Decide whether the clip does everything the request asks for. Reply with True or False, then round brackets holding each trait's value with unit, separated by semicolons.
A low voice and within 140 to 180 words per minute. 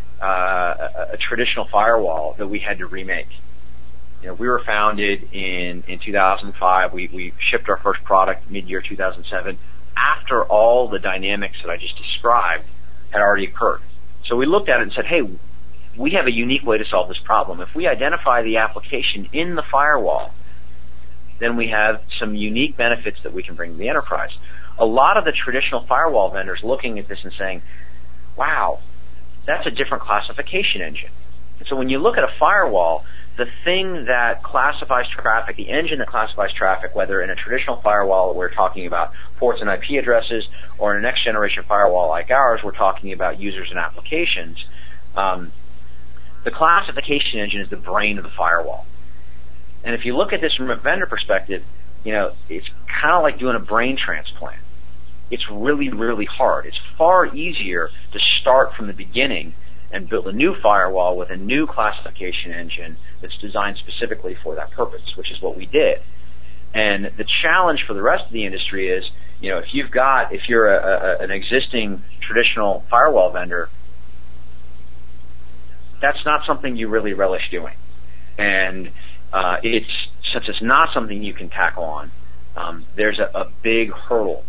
True (95 Hz; 175 wpm)